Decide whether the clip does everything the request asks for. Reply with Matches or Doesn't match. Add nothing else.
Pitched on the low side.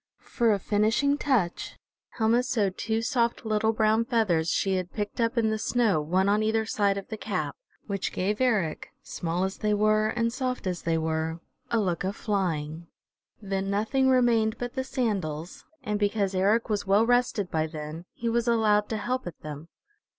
Doesn't match